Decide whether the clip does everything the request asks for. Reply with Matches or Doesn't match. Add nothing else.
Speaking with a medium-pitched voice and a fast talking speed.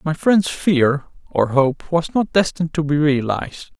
Doesn't match